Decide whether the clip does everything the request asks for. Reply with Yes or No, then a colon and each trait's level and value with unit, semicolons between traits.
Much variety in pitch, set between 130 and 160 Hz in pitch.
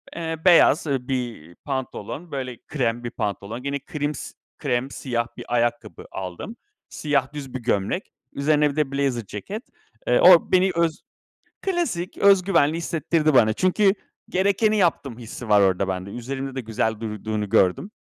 Yes: wide, 6.3 semitones; low, 135 Hz